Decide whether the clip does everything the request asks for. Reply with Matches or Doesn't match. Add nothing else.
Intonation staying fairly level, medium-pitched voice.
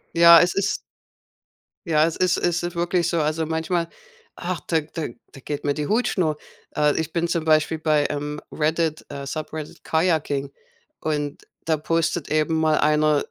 Matches